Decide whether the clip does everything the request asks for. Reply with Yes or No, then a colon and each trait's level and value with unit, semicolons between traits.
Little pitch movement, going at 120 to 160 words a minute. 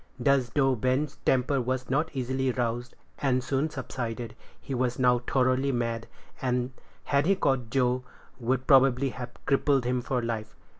Yes: narrow, 1.7 semitones; average, 155 wpm